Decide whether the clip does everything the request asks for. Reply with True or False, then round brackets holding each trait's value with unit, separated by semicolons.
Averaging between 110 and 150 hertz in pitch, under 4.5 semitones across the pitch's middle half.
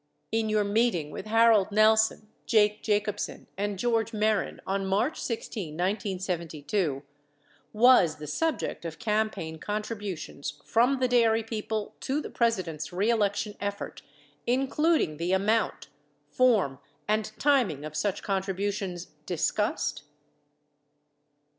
False (210 Hz; 3.5 semitones)